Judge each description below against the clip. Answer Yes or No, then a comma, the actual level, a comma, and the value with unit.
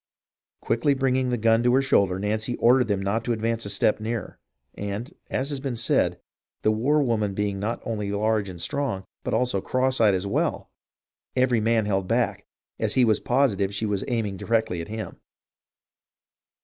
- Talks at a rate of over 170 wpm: Yes, average, 180 wpm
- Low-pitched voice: Yes, low, 110 Hz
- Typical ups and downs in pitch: Yes, average, 3.5 semitones